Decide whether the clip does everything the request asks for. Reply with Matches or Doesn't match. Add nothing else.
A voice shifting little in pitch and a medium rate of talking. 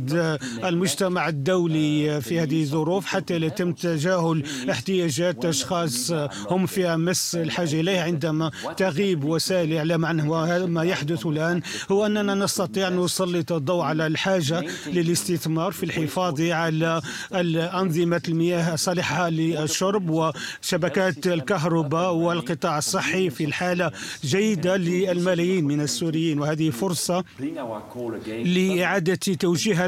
Matches